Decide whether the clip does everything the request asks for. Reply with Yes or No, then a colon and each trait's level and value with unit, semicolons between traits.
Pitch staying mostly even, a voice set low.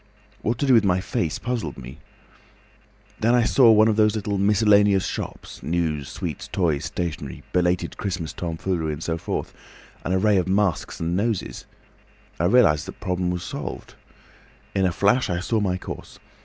No: average, 3.8 semitones; very low, 95 Hz